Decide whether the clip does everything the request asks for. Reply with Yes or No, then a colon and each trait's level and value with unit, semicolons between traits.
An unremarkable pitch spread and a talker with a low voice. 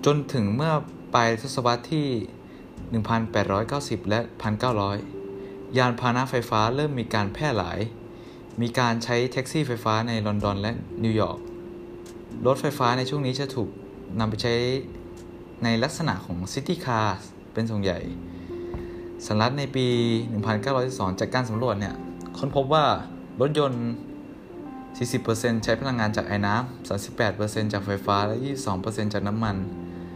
Yes: average, 4.0 semitones; low, 115 Hz